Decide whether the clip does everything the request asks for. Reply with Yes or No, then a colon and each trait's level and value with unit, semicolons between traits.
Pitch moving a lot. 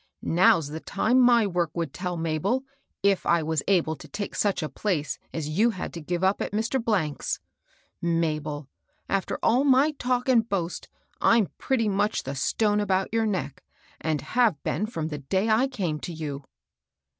Yes: wide, 5.7 semitones